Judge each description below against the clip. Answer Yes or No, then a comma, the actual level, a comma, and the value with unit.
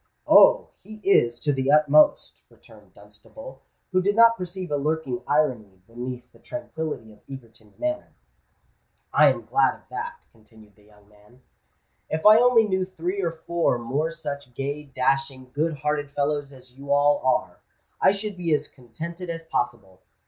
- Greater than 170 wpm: No, average, 160 wpm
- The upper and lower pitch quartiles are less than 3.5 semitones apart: No, wide, 5.5 semitones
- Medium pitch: Yes, medium, 145 Hz